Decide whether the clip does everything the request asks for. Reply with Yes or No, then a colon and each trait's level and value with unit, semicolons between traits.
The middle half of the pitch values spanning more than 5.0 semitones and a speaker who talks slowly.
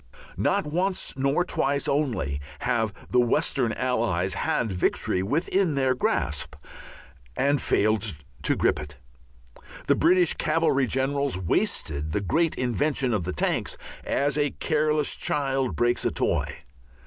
Yes: wide, 5.6 semitones; slow, 130 wpm